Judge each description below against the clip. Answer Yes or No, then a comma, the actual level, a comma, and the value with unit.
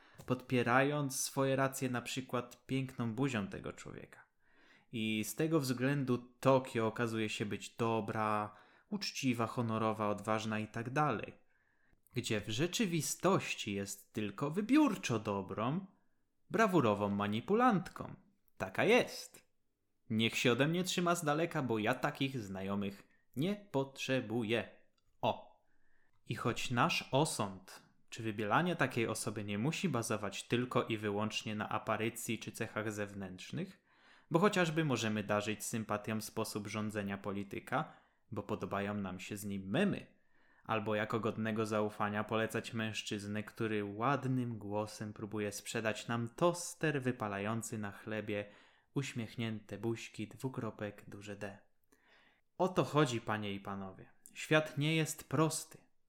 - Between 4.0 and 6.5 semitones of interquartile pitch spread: Yes, average, 4.3 semitones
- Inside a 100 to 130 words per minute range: Yes, average, 120 wpm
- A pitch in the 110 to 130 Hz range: Yes, low, 115 Hz